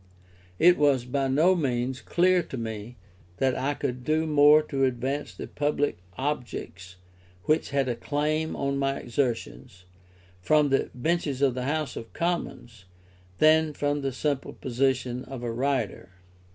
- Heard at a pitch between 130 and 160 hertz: Yes, low, 135 Hz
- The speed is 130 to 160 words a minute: Yes, average, 150 wpm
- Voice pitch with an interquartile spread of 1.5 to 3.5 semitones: Yes, average, 3.2 semitones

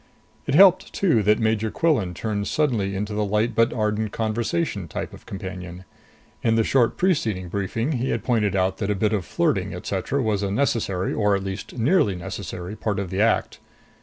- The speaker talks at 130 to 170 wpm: No, average, 190 wpm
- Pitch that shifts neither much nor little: Yes, average, 3.0 semitones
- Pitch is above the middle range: No, low, 105 Hz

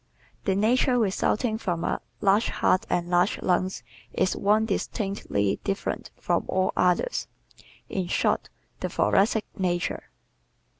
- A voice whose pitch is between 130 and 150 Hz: No, high, 195 Hz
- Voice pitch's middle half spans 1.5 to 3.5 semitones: Yes, average, 3.2 semitones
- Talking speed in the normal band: No, slow, 120 wpm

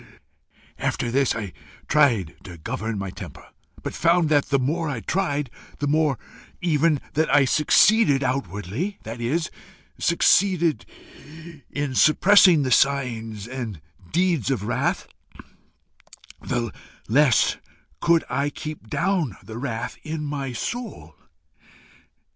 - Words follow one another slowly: Yes, slow, 120 wpm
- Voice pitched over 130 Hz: Yes, medium, 140 Hz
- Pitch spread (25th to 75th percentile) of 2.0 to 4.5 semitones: No, wide, 5.4 semitones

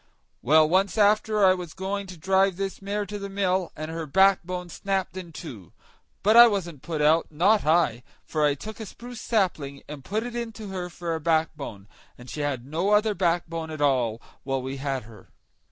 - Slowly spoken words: No, average, 200 wpm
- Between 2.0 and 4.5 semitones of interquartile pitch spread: No, average, 4.9 semitones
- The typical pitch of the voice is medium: Yes, medium, 175 Hz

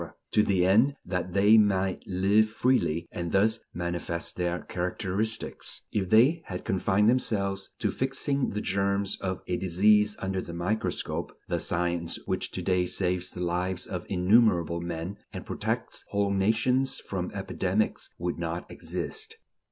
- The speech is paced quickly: No, average, 145 wpm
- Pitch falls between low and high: No, very low, 95 Hz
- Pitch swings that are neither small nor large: Yes, average, 3.2 semitones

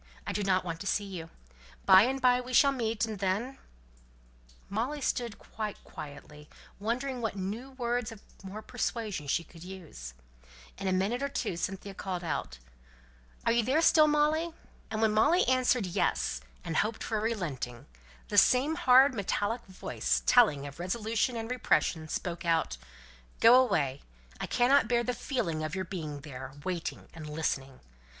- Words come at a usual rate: Yes, average, 165 wpm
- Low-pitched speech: No, high, 205 Hz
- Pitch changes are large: Yes, wide, 6.8 semitones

